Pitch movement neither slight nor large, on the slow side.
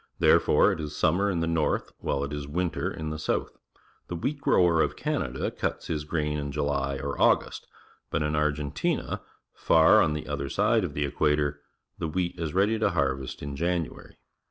No: average, 3.0 semitones; average, 185 wpm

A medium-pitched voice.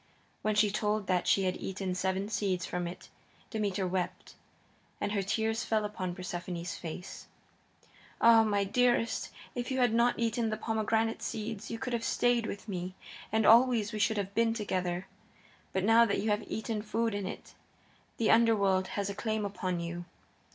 No: high, 210 Hz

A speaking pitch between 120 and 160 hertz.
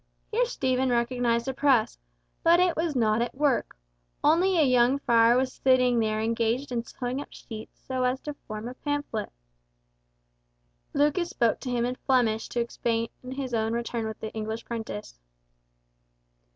No: high, 245 Hz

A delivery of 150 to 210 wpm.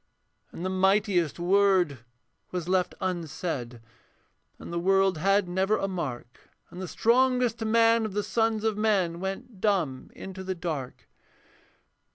No: average, 140 wpm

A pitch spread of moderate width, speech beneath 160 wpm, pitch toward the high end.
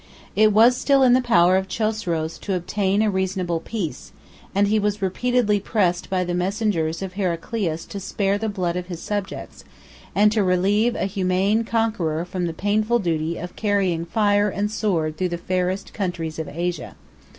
No: average, 3.2 semitones; average, 175 wpm; high, 195 Hz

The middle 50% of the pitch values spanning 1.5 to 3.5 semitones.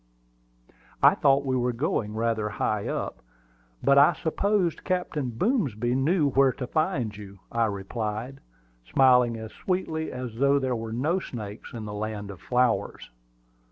No: average, 4.5 semitones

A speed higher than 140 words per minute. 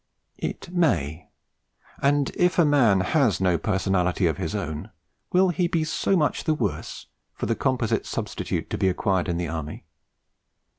Yes: average, 160 wpm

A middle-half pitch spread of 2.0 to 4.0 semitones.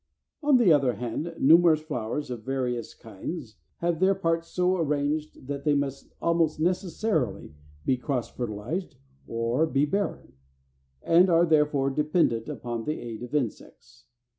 No: wide, 5.4 semitones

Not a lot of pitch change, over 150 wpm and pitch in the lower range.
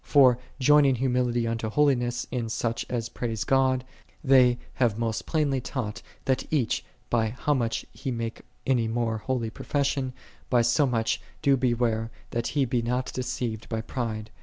Yes: narrow, 2.3 semitones; average, 160 wpm; low, 120 Hz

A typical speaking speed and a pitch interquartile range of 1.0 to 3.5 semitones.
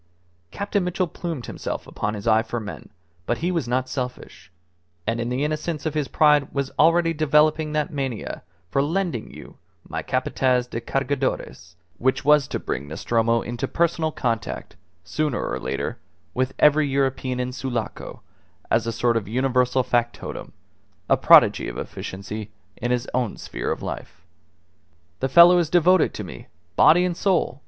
No: average, 160 wpm; average, 4.7 semitones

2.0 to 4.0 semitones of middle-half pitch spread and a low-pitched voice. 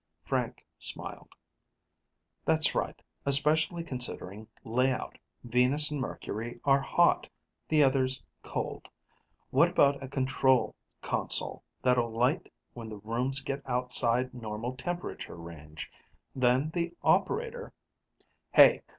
Yes: average, 3.2 semitones; low, 130 Hz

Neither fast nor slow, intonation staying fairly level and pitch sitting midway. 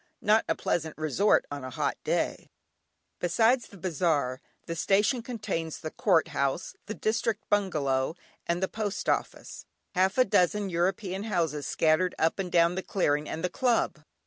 No: average, 160 wpm; average, 4.6 semitones; medium, 180 Hz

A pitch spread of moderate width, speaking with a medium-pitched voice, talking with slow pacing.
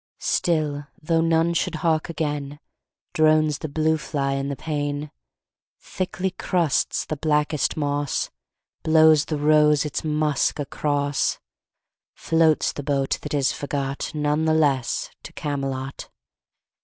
No: narrow, 1.6 semitones; medium, 150 Hz; slow, 125 wpm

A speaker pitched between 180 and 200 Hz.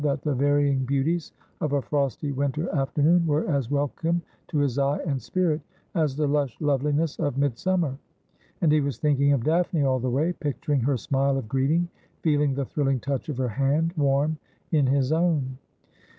No: medium, 145 Hz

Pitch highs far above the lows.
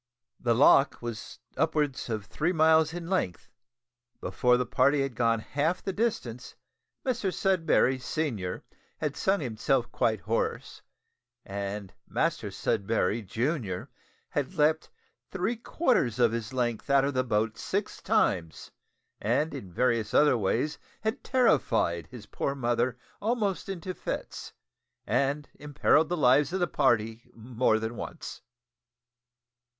Yes: wide, 6.0 semitones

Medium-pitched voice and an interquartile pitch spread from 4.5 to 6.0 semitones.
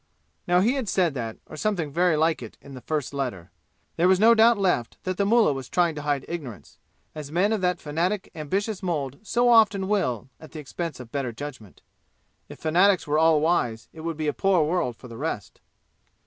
Yes: medium, 160 Hz; average, 5.3 semitones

